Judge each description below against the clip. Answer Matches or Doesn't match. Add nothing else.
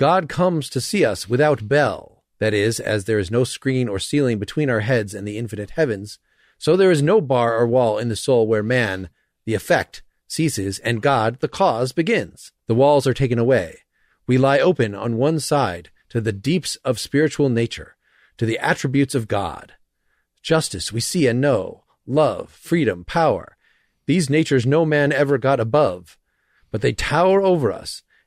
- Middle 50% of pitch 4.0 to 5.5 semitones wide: Matches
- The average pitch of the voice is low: Matches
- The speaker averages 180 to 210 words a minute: Matches